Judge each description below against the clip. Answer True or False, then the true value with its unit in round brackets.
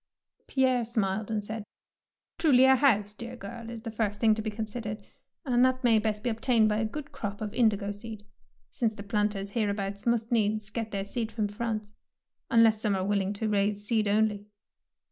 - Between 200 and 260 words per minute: True (205 wpm)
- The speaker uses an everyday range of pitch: False (2.1 semitones)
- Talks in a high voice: True (215 Hz)